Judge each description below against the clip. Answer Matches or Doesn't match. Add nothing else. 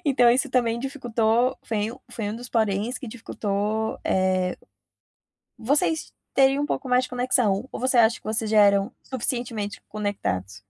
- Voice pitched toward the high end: Matches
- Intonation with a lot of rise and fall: Doesn't match